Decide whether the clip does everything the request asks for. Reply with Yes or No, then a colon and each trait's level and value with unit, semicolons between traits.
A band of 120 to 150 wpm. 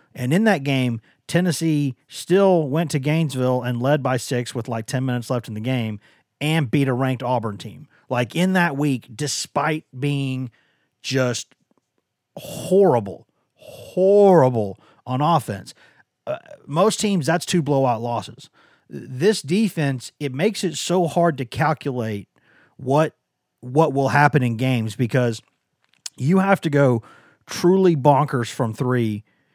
Yes: average, 140 wpm